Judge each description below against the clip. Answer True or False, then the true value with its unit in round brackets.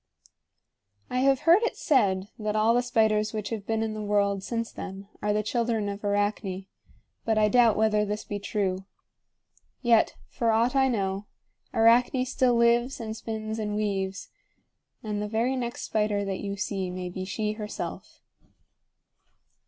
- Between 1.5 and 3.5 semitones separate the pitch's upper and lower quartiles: True (2.4 semitones)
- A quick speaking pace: False (160 wpm)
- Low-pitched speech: False (215 Hz)